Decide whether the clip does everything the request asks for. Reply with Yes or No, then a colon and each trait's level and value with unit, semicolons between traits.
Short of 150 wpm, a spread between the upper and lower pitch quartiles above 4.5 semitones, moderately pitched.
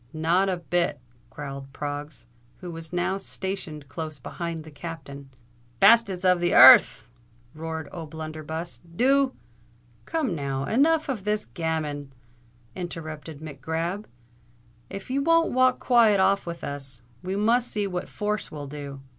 Yes: average, 140 wpm; average, 5.1 semitones; medium, 170 Hz